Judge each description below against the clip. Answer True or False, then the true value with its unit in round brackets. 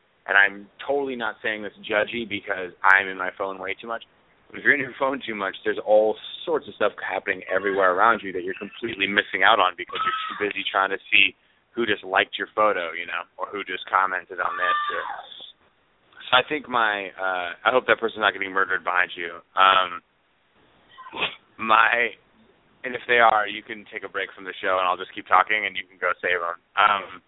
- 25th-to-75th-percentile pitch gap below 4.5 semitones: False (5.5 semitones)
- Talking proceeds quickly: True (215 wpm)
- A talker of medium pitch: False (100 Hz)